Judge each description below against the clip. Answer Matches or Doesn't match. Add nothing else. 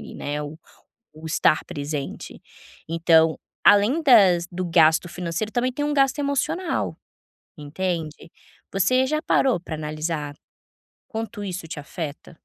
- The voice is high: Doesn't match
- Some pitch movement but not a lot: Doesn't match